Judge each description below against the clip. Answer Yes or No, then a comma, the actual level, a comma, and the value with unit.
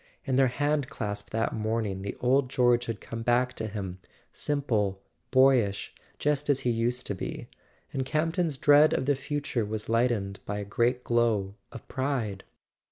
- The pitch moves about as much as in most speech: Yes, average, 4.3 semitones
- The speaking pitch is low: Yes, low, 120 Hz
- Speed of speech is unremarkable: Yes, average, 170 wpm